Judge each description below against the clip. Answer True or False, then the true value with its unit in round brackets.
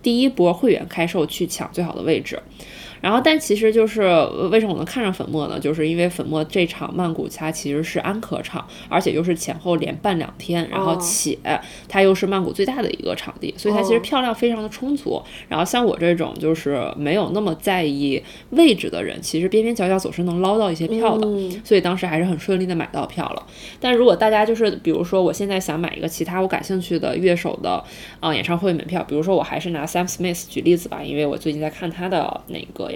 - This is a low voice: False (175 Hz)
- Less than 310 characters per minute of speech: False (355 characters per minute)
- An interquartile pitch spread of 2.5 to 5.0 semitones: True (4.0 semitones)